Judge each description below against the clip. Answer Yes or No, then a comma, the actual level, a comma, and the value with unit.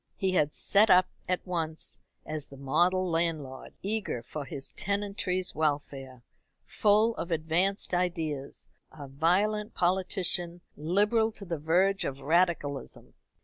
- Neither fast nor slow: No, slow, 125 wpm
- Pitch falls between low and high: Yes, medium, 175 Hz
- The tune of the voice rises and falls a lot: No, average, 4.2 semitones